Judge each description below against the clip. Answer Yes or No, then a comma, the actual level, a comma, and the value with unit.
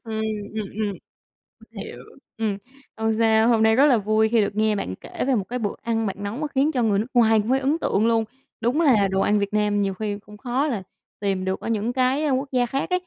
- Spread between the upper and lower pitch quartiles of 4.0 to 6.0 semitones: No, average, 3.3 semitones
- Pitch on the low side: No, high, 220 Hz